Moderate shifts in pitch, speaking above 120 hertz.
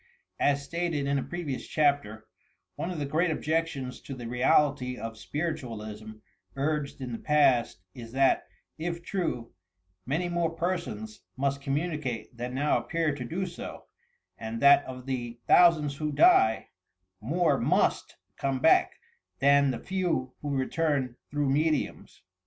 Yes: average, 4.1 semitones; medium, 140 Hz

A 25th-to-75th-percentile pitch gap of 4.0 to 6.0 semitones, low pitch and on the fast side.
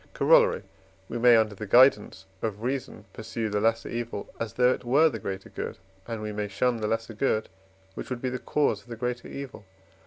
No: average, 2.8 semitones; low, 115 Hz; fast, 210 wpm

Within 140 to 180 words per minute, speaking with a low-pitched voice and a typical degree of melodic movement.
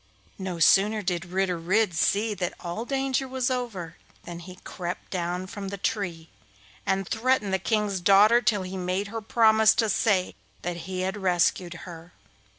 No: average, 165 wpm; high, 190 Hz; average, 3.5 semitones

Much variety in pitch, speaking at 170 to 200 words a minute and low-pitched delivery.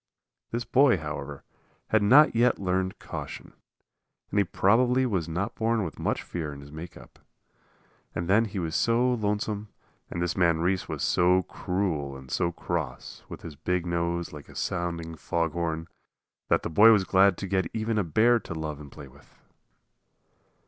No: average, 4.6 semitones; average, 175 wpm; very low, 90 Hz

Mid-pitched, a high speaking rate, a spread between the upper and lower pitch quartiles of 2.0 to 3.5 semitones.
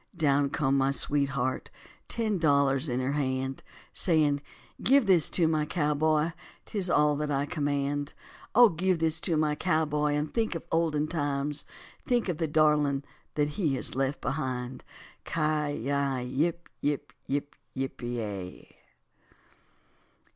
No: medium, 150 Hz; average, 140 wpm; narrow, 2.6 semitones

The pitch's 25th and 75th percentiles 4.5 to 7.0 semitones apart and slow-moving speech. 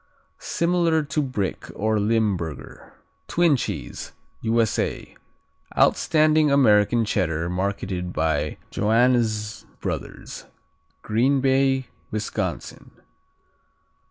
Yes: wide, 5.5 semitones; slow, 75 wpm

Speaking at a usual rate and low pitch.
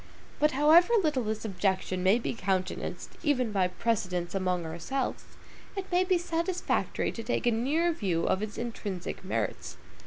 No: average, 155 wpm; high, 225 Hz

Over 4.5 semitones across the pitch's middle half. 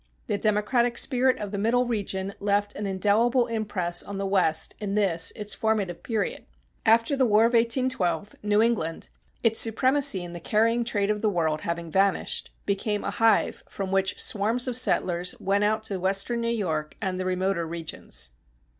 No: average, 3.4 semitones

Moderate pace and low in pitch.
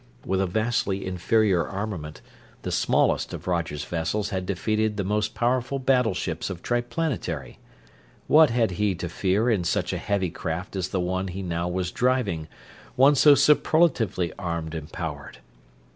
Yes: average, 155 wpm; very low, 95 Hz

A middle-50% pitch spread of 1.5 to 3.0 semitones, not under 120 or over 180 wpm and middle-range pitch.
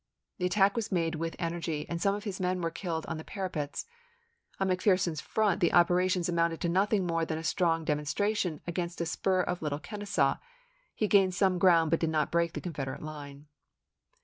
No: narrow, 2.6 semitones; average, 200 wpm; medium, 175 Hz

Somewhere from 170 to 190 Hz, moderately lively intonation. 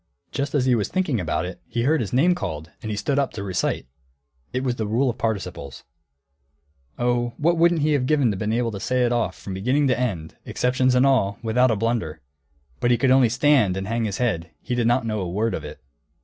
No: low, 120 Hz; average, 4.3 semitones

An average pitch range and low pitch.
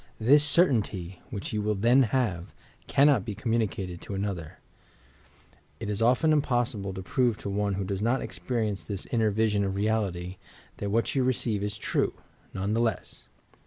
Yes: average, 3.4 semitones; low, 105 Hz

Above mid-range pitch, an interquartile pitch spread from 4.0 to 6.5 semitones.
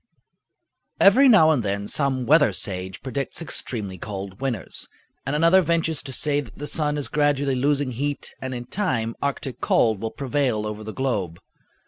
No: low, 135 Hz; average, 5.2 semitones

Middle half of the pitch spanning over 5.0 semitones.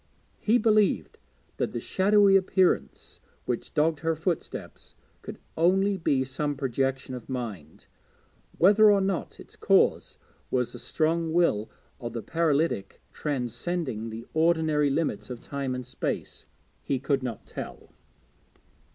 Yes: wide, 5.4 semitones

